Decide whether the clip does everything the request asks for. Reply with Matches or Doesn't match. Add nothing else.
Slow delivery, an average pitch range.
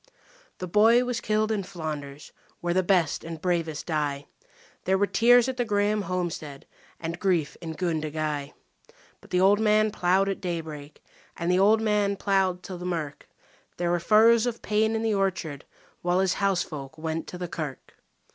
Doesn't match